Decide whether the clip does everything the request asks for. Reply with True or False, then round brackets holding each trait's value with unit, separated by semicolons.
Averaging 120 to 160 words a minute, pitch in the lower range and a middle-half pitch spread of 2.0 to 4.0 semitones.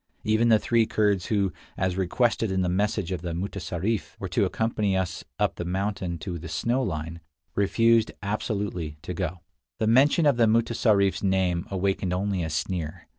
False (175 wpm; 95 Hz; 3.6 semitones)